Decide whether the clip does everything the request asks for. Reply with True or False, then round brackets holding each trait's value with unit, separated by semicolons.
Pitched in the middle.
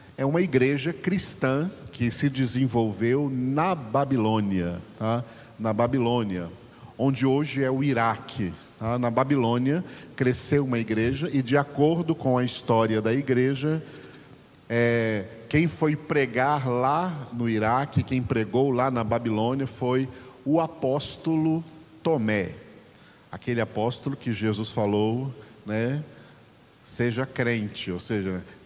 False (125 Hz)